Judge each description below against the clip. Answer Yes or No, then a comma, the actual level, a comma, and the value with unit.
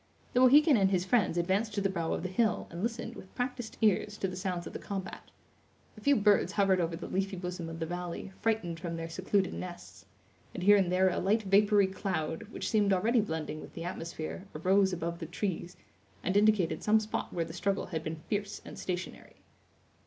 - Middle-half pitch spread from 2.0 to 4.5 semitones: Yes, average, 3.2 semitones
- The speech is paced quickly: Yes, fast, 210 wpm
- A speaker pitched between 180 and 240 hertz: Yes, high, 190 Hz